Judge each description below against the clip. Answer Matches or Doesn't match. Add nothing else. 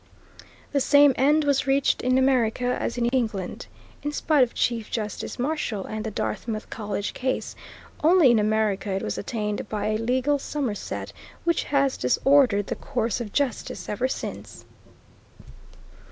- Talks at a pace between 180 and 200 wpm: Doesn't match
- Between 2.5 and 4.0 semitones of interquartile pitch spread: Doesn't match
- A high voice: Matches